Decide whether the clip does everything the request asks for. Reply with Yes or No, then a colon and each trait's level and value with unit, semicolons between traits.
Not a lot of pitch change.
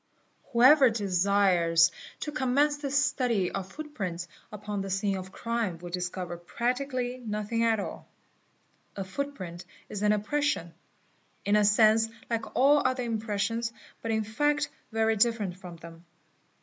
No: average, 4.7 semitones